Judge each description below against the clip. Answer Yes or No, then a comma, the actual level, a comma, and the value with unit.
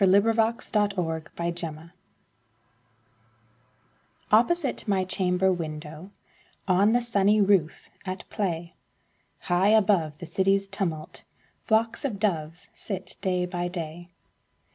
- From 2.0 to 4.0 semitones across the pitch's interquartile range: Yes, average, 3.4 semitones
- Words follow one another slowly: Yes, slow, 110 wpm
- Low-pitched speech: No, medium, 185 Hz